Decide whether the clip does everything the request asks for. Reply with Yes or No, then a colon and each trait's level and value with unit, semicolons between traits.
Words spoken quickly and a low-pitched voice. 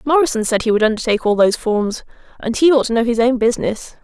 No: fast, 240 wpm; high, 235 Hz